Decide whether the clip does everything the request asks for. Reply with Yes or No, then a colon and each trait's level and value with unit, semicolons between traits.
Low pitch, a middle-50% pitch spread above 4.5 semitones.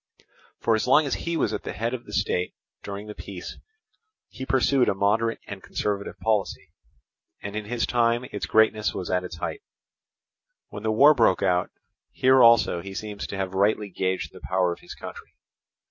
No: low, 105 Hz; average, 3.4 semitones